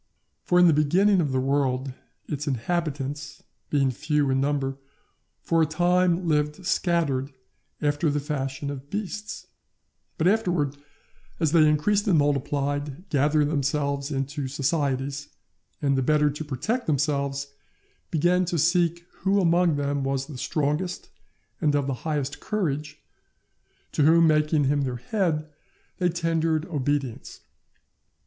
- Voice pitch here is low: No, medium, 150 Hz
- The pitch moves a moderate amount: Yes, average, 3.2 semitones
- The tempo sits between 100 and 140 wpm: Yes, slow, 135 wpm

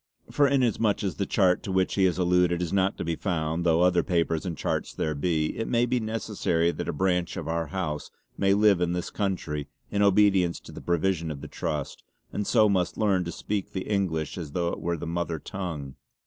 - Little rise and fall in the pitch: No, average, 3.1 semitones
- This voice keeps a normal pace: No, fast, 220 wpm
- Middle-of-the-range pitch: No, very low, 90 Hz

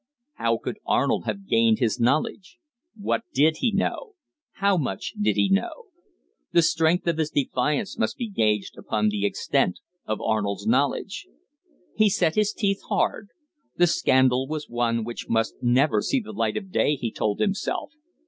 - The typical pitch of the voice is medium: Yes, medium, 145 Hz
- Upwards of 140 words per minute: Yes, average, 165 wpm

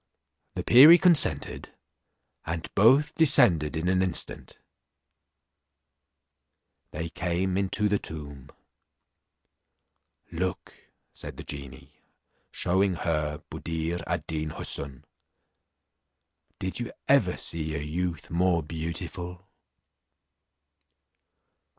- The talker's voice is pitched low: Yes, very low, 85 Hz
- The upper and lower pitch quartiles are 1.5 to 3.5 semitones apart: Yes, average, 3.2 semitones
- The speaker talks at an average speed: No, slow, 90 wpm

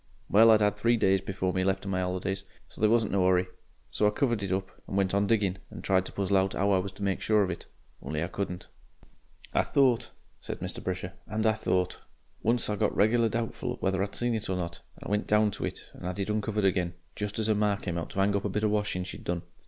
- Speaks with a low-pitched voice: Yes, low, 100 Hz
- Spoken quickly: Yes, fast, 260 wpm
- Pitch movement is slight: Yes, narrow, 2.3 semitones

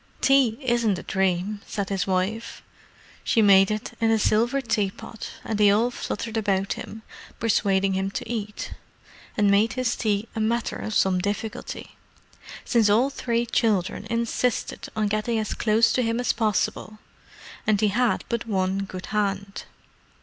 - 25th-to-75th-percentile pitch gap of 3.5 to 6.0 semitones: No, narrow, 2.5 semitones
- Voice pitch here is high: Yes, high, 215 Hz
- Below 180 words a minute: Yes, average, 160 wpm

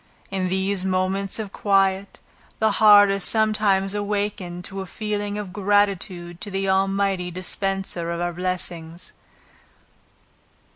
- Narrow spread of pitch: Yes, narrow, 1.8 semitones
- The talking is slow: Yes, slow, 125 wpm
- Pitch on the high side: Yes, high, 195 Hz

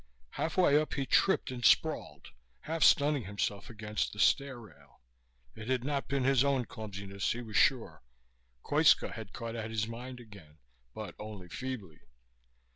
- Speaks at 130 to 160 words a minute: Yes, average, 155 wpm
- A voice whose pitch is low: Yes, low, 115 Hz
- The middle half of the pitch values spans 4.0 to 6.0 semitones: Yes, average, 4.5 semitones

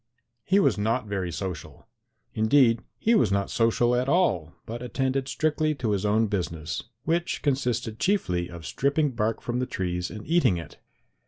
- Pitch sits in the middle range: No, low, 115 Hz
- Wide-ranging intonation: Yes, wide, 5.8 semitones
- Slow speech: No, average, 165 wpm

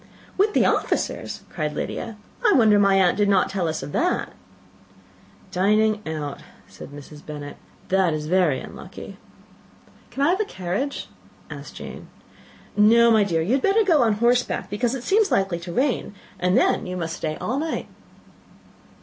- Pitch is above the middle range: Yes, high, 200 Hz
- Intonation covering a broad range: Yes, wide, 6.2 semitones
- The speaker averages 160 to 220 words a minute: Yes, average, 165 wpm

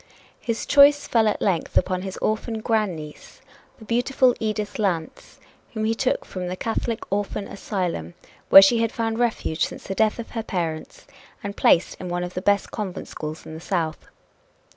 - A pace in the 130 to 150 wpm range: No, average, 180 wpm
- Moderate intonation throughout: Yes, average, 4.0 semitones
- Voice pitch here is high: Yes, high, 205 Hz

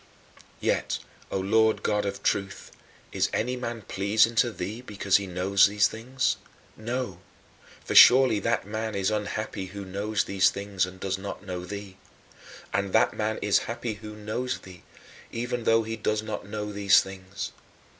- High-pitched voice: No, low, 105 Hz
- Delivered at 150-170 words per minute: Yes, average, 165 wpm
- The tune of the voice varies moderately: No, narrow, 2.3 semitones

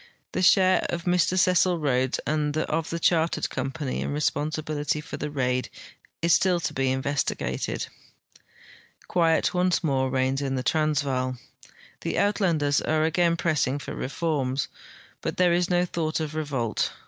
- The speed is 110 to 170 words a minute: Yes, average, 150 wpm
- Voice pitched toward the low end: No, medium, 155 Hz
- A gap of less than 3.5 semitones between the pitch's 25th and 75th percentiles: No, average, 3.9 semitones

